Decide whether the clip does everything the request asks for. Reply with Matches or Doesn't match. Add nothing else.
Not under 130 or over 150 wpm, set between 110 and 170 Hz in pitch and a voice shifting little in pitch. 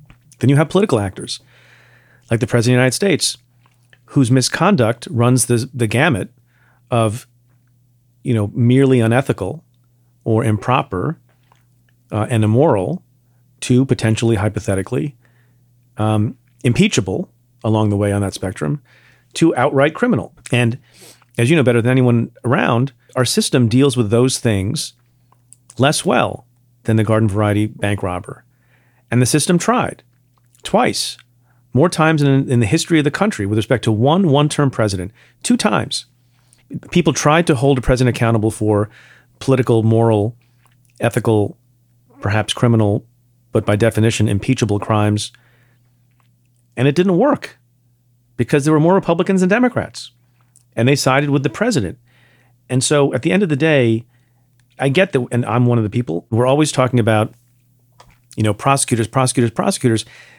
Matches